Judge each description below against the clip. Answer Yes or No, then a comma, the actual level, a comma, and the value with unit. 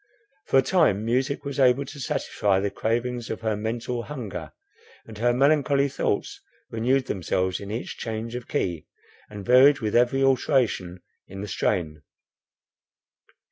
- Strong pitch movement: No, average, 4.5 semitones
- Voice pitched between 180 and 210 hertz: No, low, 120 Hz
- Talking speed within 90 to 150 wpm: Yes, average, 145 wpm